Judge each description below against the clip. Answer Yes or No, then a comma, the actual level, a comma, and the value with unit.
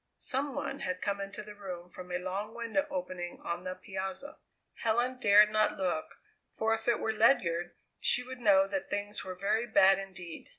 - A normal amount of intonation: Yes, average, 3.4 semitones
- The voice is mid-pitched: No, high, 200 Hz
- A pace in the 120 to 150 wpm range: No, average, 185 wpm